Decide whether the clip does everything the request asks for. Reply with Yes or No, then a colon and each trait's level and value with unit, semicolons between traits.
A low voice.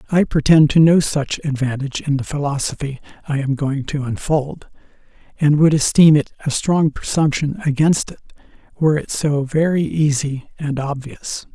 No: medium, 145 Hz